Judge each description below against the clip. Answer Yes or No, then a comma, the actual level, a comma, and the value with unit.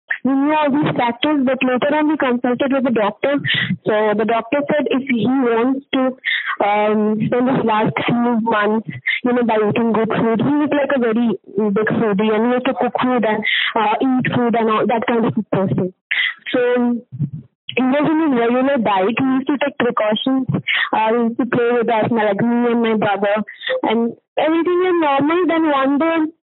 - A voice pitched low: No, high, 240 Hz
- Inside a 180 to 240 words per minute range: Yes, average, 195 wpm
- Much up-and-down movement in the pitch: No, average, 4.0 semitones